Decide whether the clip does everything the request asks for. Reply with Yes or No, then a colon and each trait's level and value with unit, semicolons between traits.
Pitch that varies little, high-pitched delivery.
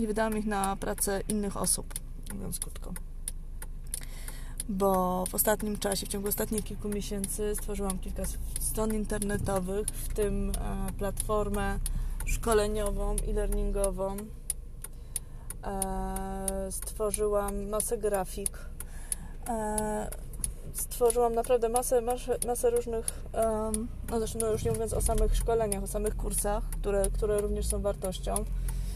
Yes: narrow, 1.7 semitones; high, 205 Hz